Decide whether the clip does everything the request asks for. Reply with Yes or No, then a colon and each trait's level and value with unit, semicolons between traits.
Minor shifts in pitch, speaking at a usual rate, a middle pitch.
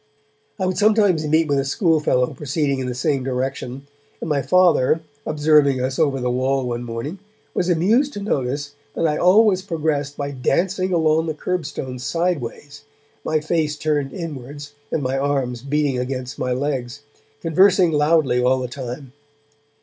No: average, 3.9 semitones; average, 155 wpm; medium, 145 Hz